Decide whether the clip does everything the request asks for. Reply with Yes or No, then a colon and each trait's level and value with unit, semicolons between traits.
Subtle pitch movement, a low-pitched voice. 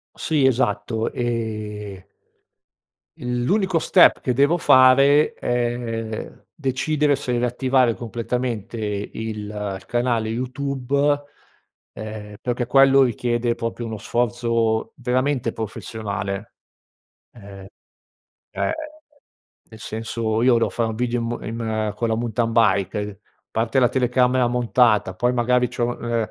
Yes: narrow, 2.3 semitones; low, 120 Hz